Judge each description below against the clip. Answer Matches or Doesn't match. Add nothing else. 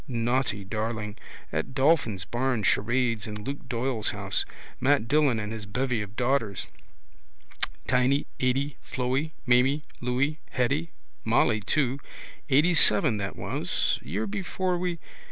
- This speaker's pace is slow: Matches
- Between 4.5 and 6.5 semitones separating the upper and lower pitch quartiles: Doesn't match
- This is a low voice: Matches